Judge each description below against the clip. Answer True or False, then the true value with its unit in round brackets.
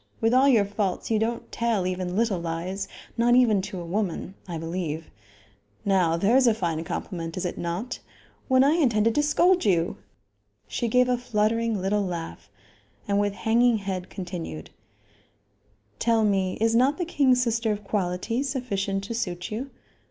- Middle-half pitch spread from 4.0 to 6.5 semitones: True (4.5 semitones)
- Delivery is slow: False (165 wpm)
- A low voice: False (210 Hz)